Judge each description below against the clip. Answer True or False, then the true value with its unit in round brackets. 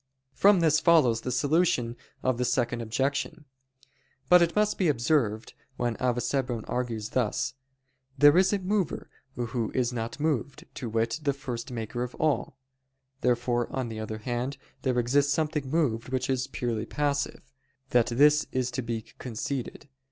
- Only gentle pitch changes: False (3.6 semitones)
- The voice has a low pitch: True (125 Hz)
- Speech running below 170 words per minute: True (155 wpm)